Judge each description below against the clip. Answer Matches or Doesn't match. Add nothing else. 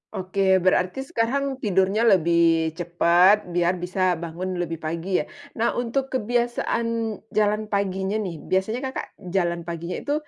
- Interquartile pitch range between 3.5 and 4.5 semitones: Matches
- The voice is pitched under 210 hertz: Matches